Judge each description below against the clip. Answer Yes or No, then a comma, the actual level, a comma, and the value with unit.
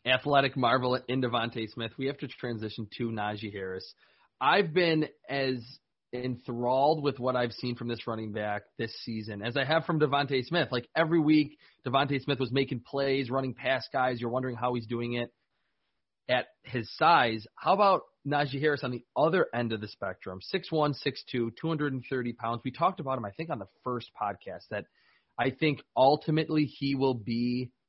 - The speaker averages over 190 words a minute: No, average, 180 wpm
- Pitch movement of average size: Yes, average, 3.1 semitones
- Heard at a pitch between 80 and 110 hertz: No, low, 130 Hz